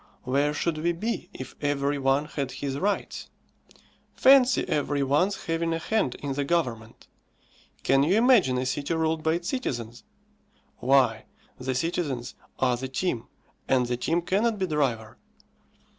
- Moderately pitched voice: Yes, medium, 145 Hz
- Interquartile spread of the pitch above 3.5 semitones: Yes, average, 4.7 semitones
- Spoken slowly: No, average, 150 wpm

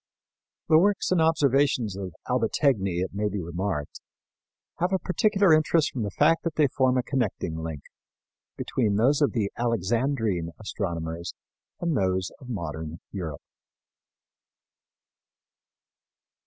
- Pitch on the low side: Yes, low, 110 Hz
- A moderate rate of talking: No, slow, 125 wpm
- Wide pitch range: Yes, wide, 7.8 semitones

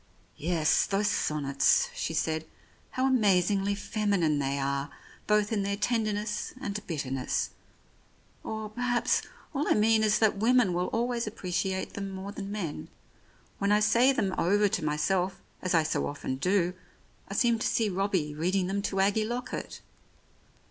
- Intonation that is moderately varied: Yes, average, 3.9 semitones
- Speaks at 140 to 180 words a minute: Yes, average, 160 wpm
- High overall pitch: Yes, high, 200 Hz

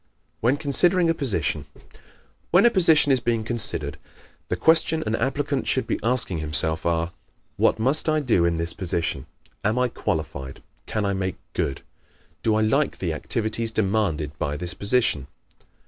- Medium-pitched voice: No, low, 110 Hz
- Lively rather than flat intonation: Yes, wide, 8.1 semitones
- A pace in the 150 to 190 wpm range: Yes, average, 160 wpm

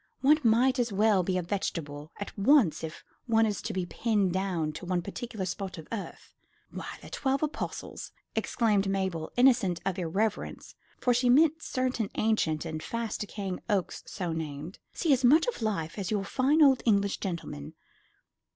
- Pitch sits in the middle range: No, high, 200 Hz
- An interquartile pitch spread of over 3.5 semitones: Yes, average, 5.2 semitones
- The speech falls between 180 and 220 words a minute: No, average, 170 wpm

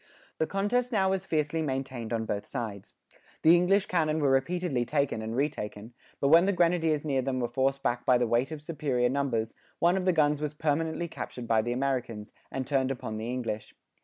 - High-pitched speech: No, medium, 140 Hz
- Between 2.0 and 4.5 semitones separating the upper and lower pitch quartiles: No, average, 4.9 semitones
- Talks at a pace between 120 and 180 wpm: No, average, 200 wpm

